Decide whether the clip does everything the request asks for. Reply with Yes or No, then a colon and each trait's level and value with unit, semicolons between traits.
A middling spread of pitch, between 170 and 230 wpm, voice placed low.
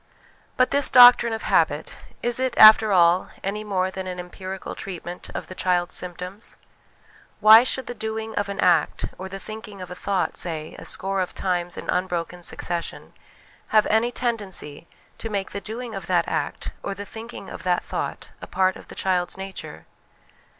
No: average, 3.4 semitones; average, 180 wpm; high, 195 Hz